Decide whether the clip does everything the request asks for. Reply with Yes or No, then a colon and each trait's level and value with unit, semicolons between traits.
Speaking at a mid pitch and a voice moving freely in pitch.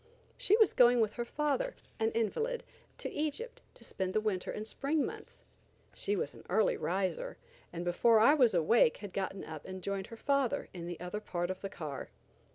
No: high, 215 Hz; wide, 7.1 semitones